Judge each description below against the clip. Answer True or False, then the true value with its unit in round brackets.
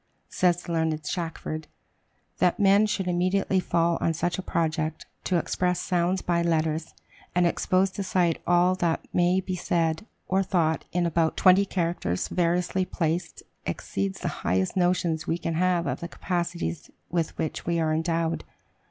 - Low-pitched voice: False (170 Hz)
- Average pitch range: False (1.9 semitones)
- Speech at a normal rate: True (160 wpm)